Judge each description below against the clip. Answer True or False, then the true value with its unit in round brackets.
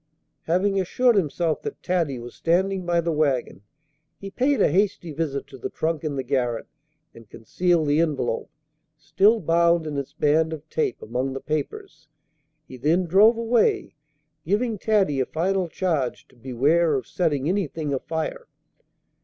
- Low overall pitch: False (160 Hz)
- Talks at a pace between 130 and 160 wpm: True (155 wpm)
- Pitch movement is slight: False (4.8 semitones)